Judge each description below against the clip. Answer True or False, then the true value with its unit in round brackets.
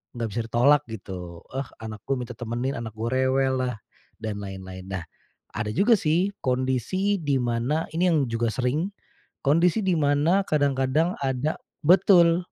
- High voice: False (130 Hz)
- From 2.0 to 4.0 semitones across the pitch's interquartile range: False (5.5 semitones)